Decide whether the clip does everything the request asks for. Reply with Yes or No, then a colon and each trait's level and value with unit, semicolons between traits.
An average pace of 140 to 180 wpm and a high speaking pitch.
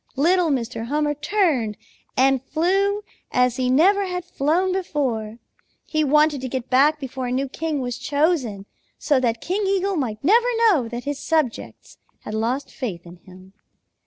Yes: average, 160 wpm; very high, 280 Hz